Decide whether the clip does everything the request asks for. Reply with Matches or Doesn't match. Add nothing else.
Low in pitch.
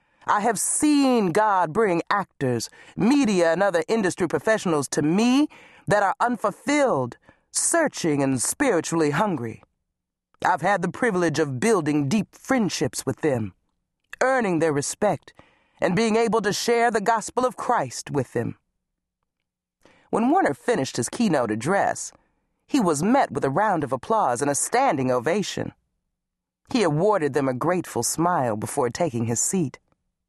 Doesn't match